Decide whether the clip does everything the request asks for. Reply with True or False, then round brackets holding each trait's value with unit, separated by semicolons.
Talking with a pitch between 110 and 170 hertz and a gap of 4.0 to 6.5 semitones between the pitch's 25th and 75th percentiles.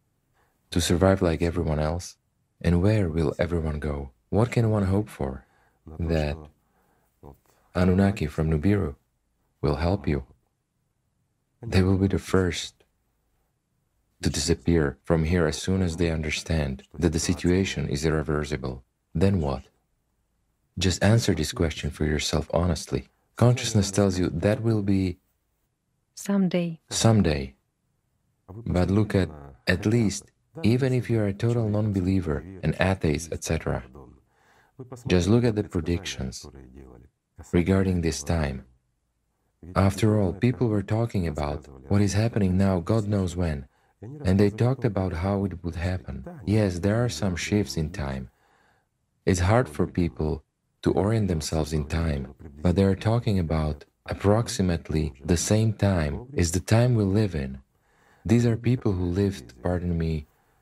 False (90 Hz; 5.0 semitones)